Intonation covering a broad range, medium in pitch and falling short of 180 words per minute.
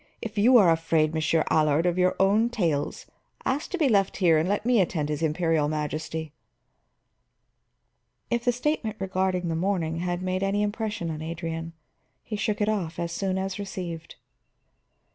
No: average, 4.2 semitones; medium, 180 Hz; average, 165 wpm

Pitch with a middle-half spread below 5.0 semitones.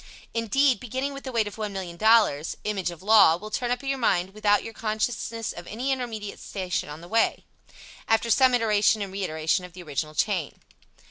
Yes: average, 4.2 semitones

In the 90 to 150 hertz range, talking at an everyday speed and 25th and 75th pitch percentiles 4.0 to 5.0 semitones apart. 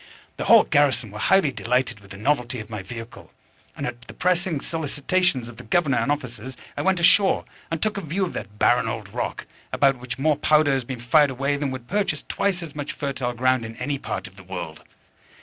No: low, 135 Hz; fast, 220 wpm; average, 4.6 semitones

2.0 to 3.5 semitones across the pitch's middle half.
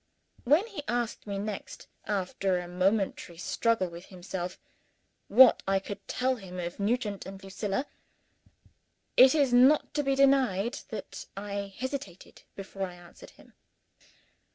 No: average, 5.0 semitones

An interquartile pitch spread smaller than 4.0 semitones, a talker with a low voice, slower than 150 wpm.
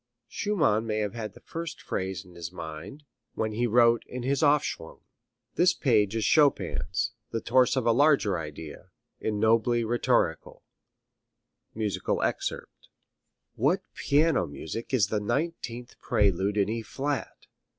No: average, 4.7 semitones; low, 115 Hz; average, 140 wpm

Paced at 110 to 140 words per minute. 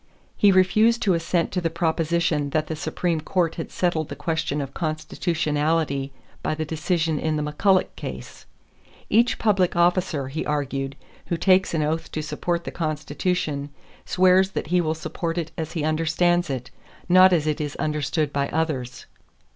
No: average, 165 wpm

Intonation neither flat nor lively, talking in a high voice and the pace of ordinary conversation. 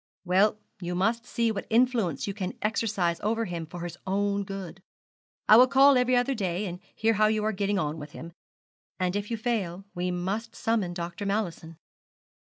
Yes: average, 4.1 semitones; high, 200 Hz; average, 190 wpm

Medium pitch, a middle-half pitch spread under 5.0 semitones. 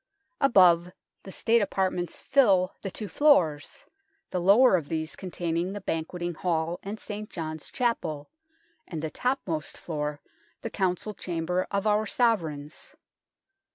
Yes: medium, 180 Hz; average, 4.3 semitones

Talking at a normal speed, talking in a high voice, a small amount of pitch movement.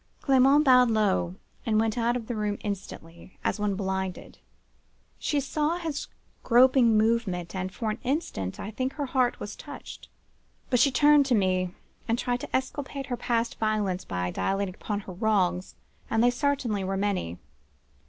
No: average, 165 wpm; high, 220 Hz; average, 5.0 semitones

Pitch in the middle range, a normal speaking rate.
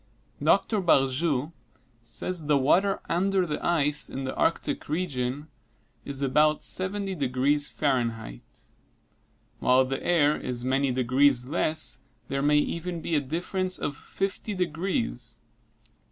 No: medium, 145 Hz; slow, 125 wpm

